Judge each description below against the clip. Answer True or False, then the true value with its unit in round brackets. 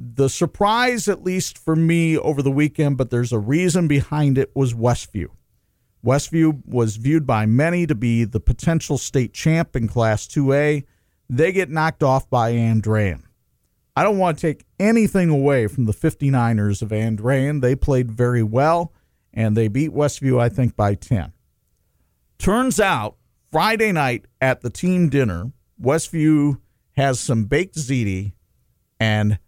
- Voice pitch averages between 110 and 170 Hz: True (135 Hz)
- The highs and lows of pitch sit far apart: True (5.7 semitones)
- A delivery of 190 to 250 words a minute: False (155 wpm)